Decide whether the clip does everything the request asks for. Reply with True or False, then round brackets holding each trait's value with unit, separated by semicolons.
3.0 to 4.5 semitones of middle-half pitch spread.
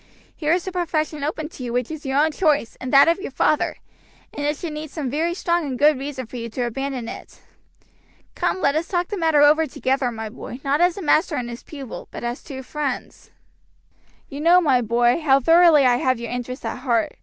True (4.0 semitones)